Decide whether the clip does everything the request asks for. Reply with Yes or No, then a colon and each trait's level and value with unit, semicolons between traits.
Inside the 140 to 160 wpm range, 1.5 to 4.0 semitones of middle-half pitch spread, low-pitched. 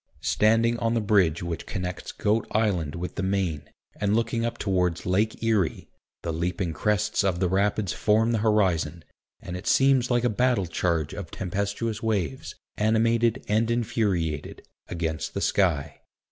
No: average, 155 wpm; average, 4.4 semitones; low, 100 Hz